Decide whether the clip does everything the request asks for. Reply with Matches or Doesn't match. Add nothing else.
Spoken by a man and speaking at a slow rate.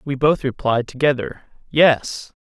Matches